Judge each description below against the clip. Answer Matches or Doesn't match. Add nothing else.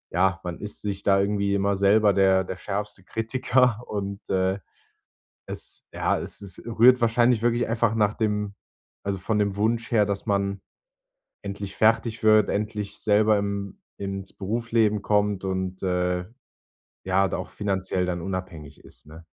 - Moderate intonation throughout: Doesn't match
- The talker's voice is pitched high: Doesn't match